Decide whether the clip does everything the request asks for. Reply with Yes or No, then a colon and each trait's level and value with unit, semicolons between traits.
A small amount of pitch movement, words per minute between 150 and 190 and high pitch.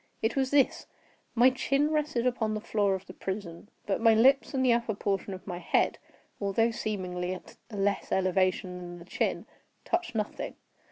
No: average, 4.7 semitones; average, 180 wpm; high, 215 Hz